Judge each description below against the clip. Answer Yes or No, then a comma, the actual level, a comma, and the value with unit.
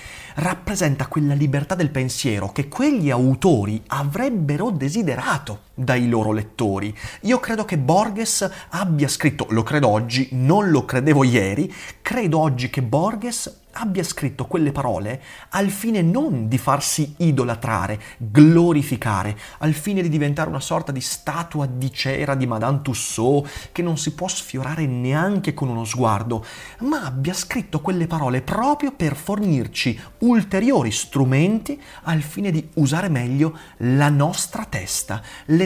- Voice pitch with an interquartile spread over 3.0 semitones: Yes, wide, 5.6 semitones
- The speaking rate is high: No, average, 140 wpm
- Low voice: No, medium, 145 Hz